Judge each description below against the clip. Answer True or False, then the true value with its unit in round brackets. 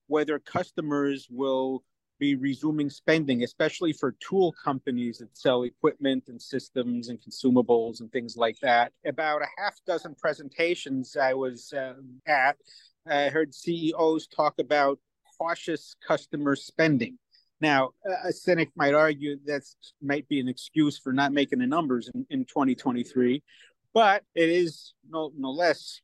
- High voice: False (140 Hz)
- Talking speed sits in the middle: True (145 wpm)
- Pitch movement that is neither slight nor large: True (3.4 semitones)